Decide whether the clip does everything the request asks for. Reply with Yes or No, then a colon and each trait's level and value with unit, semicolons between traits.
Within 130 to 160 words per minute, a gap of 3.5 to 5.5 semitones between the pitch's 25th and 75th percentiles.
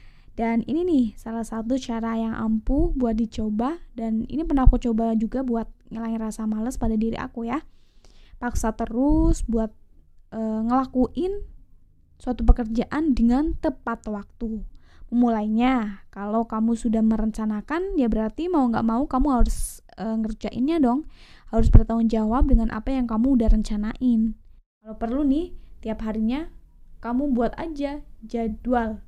No: fast, 140 wpm; average, 2.8 semitones